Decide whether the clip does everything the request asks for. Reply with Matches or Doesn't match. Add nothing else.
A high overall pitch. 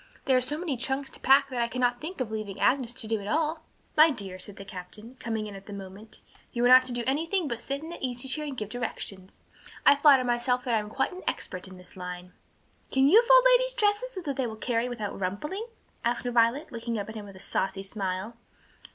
Matches